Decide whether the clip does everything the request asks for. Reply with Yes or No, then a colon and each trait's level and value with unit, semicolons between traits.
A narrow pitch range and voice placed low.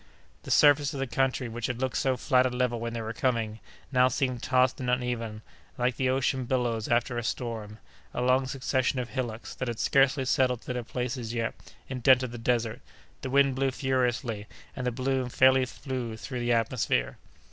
Yes: narrow, 1.9 semitones; low, 125 Hz